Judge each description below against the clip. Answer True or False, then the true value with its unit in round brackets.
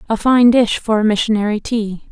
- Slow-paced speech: False (200 wpm)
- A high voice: True (220 Hz)